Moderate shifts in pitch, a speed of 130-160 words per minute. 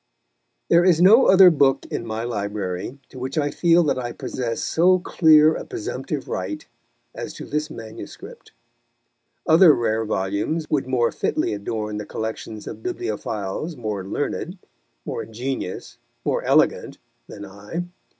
No: wide, 7.7 semitones; average, 140 wpm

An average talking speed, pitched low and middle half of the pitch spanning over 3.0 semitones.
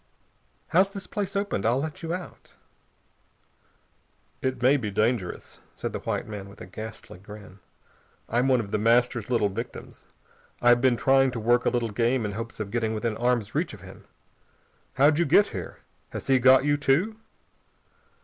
Yes: average, 175 wpm; low, 120 Hz; average, 3.9 semitones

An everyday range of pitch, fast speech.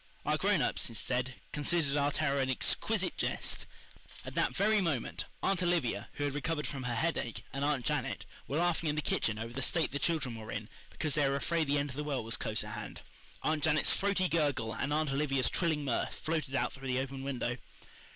Yes: average, 3.3 semitones; fast, 215 wpm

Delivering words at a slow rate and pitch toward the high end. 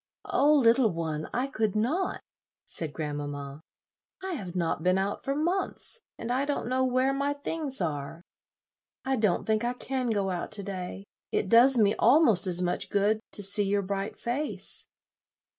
No: average, 170 wpm; high, 215 Hz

